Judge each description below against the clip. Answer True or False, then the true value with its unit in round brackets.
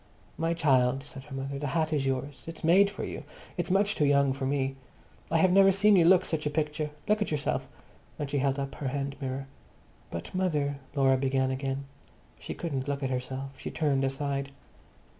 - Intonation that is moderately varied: True (3.1 semitones)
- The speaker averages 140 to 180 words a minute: False (200 wpm)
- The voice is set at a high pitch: False (140 Hz)